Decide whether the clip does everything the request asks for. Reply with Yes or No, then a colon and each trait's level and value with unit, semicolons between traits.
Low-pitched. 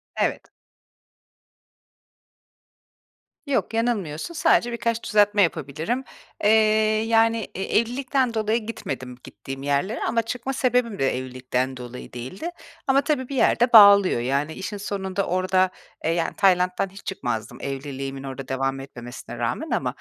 No: high, 190 Hz